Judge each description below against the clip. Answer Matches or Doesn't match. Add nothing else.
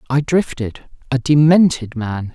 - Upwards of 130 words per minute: Doesn't match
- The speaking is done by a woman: Doesn't match